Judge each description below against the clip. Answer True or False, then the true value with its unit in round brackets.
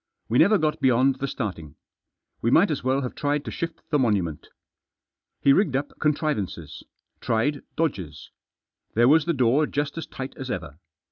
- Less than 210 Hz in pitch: True (135 Hz)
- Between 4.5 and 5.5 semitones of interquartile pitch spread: True (4.9 semitones)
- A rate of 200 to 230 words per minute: False (165 wpm)